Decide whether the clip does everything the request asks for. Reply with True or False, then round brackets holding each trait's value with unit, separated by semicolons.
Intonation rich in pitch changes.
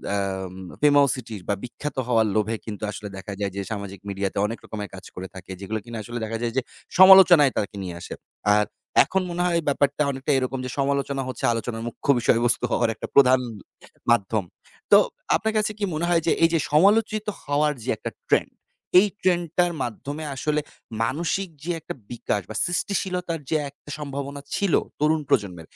True (6.9 semitones)